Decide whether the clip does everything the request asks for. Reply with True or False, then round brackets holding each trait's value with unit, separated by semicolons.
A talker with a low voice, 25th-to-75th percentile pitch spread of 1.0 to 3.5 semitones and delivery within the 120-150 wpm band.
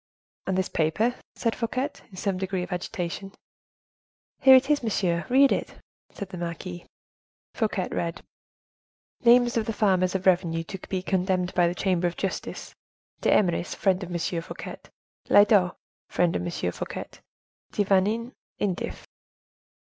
False (190 Hz; 3.2 semitones; 140 wpm)